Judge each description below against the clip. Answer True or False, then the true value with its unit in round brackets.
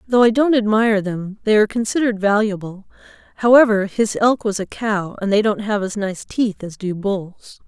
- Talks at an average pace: True (195 wpm)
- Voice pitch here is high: True (210 Hz)